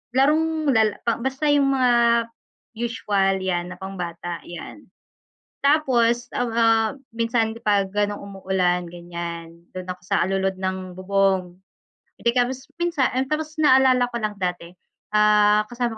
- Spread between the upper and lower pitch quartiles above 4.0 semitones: Yes, average, 4.9 semitones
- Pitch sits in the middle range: No, high, 210 Hz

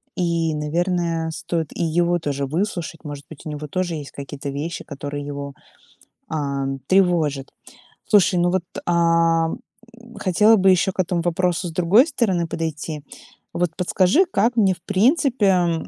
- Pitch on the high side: No, medium, 170 Hz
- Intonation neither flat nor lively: Yes, average, 3.5 semitones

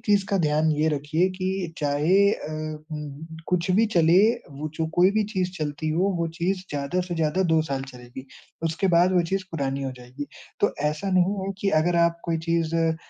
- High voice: No, medium, 165 Hz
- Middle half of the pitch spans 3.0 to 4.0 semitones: Yes, average, 3.6 semitones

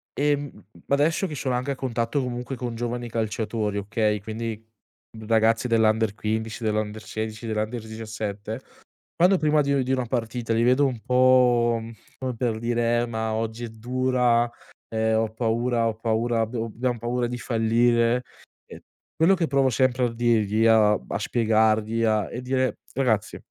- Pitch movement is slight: Yes, narrow, 2.2 semitones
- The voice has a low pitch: Yes, low, 115 Hz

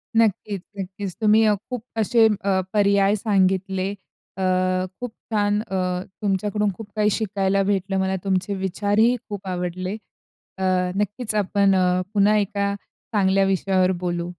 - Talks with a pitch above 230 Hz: No, high, 200 Hz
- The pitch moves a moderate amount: No, narrow, 1.6 semitones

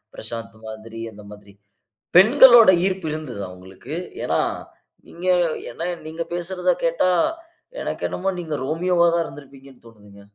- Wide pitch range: Yes, wide, 8.6 semitones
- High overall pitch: No, medium, 150 Hz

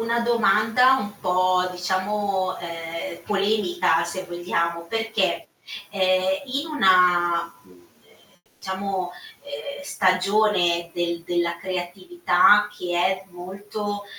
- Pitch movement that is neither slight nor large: Yes, average, 3.1 semitones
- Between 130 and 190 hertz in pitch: Yes, medium, 185 Hz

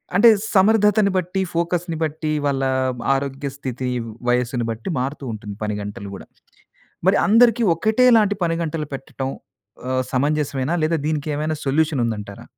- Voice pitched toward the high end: No, medium, 150 Hz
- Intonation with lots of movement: Yes, wide, 5.7 semitones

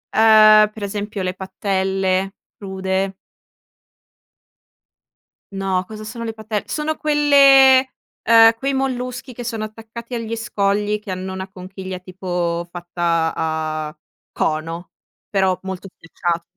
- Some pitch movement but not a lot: Yes, average, 3.5 semitones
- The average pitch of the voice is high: Yes, high, 195 Hz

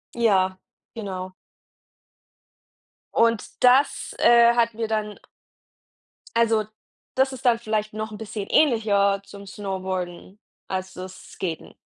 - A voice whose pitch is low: No, high, 215 Hz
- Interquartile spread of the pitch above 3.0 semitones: Yes, average, 3.5 semitones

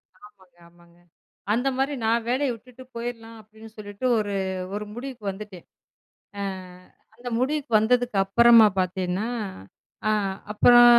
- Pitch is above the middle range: Yes, high, 225 Hz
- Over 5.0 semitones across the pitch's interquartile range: No, average, 3.3 semitones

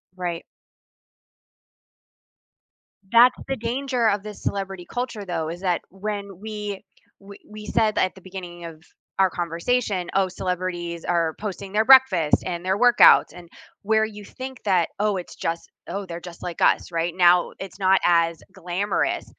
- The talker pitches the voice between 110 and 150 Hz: No, high, 190 Hz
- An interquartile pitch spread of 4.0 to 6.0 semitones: No, average, 3.3 semitones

